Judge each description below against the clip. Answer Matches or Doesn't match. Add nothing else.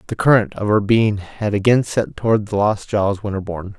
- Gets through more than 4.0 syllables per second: Matches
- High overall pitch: Doesn't match